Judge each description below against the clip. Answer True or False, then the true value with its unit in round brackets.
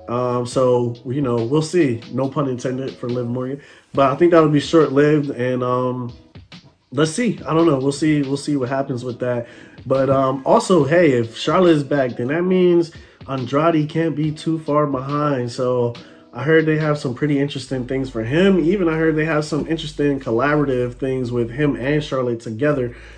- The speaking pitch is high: False (140 Hz)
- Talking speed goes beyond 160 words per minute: True (195 wpm)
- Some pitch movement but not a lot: True (3.7 semitones)